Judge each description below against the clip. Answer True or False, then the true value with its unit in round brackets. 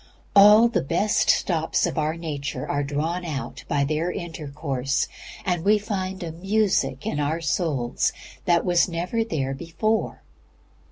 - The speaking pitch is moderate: True (165 Hz)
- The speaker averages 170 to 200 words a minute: False (145 wpm)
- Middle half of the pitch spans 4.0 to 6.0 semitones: True (4.5 semitones)